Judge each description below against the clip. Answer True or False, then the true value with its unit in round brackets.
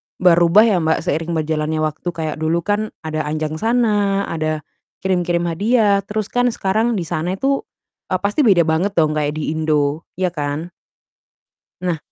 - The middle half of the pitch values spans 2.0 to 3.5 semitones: False (4.3 semitones)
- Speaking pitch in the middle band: True (170 Hz)